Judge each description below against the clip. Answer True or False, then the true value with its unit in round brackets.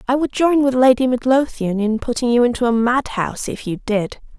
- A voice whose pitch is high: True (245 Hz)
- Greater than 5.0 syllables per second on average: True (5.4 syllables/s)